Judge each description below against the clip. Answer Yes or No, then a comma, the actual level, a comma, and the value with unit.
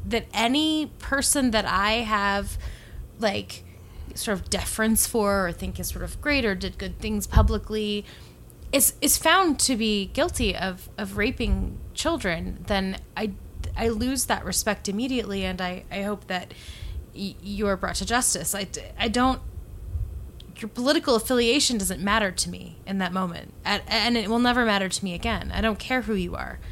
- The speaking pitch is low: No, high, 210 Hz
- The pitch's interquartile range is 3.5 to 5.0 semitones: Yes, average, 4.6 semitones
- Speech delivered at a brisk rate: No, average, 175 wpm